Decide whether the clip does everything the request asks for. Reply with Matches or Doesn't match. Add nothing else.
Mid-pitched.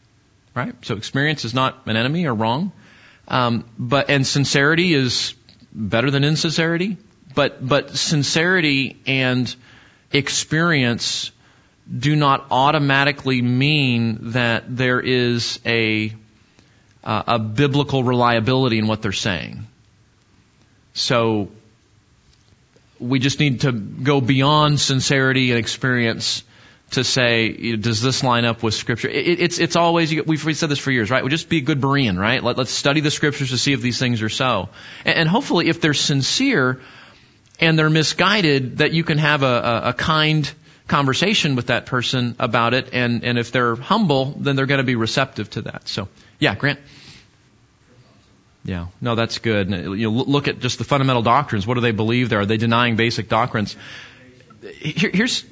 Doesn't match